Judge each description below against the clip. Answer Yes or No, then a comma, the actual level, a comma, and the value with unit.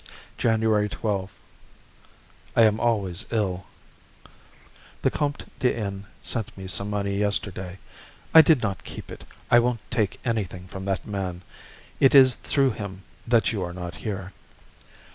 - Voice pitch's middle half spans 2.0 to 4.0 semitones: Yes, average, 3.3 semitones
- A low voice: Yes, low, 105 Hz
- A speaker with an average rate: Yes, average, 145 wpm